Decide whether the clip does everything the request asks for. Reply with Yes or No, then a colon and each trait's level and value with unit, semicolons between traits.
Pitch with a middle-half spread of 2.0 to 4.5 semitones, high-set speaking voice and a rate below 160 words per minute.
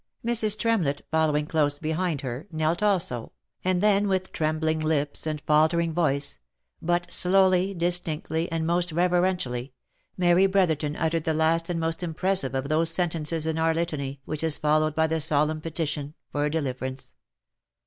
No: narrow, 2.6 semitones; medium, 160 Hz; average, 150 wpm